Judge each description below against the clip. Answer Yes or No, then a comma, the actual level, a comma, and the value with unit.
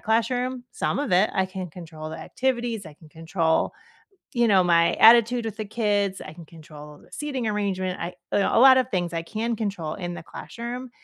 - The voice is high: Yes, high, 200 Hz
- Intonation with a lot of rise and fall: Yes, wide, 5.7 semitones